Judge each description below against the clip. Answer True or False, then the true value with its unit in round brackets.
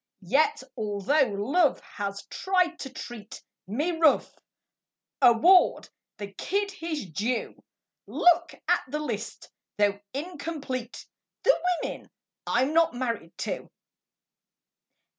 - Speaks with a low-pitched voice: False (270 Hz)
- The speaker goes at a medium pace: False (105 wpm)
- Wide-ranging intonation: True (7.6 semitones)